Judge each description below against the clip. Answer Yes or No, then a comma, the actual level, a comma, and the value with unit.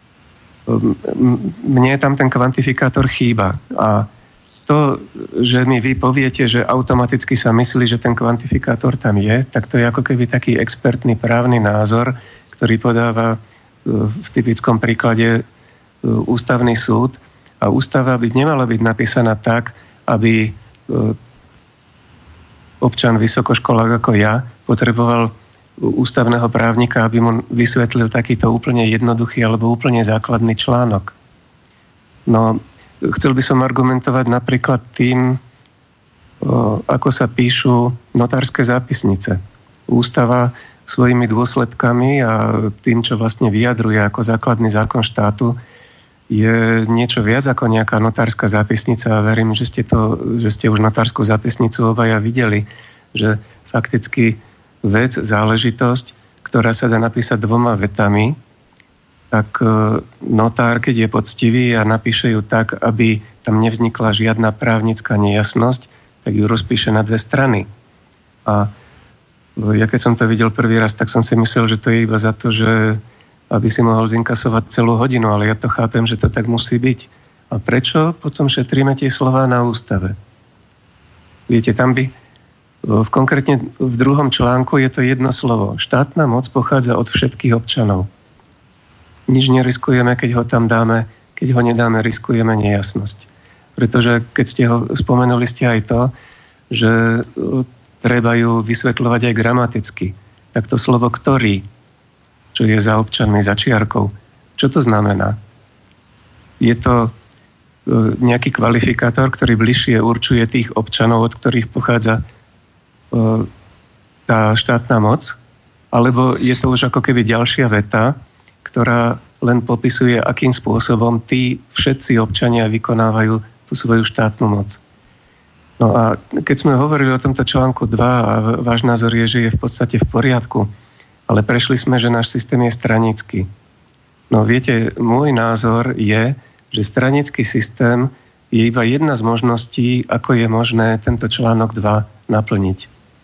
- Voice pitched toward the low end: Yes, low, 115 Hz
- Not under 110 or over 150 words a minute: Yes, average, 135 wpm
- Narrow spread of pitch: Yes, narrow, 2.0 semitones